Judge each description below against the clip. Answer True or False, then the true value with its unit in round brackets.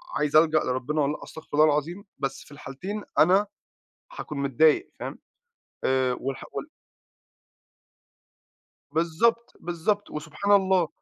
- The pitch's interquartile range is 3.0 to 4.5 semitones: False (5.0 semitones)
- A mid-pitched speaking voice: True (155 Hz)